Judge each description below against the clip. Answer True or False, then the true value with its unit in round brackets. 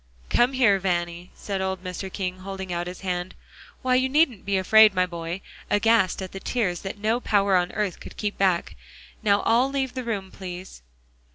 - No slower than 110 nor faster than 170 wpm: False (190 wpm)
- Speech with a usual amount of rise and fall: True (3.3 semitones)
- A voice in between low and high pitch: False (195 Hz)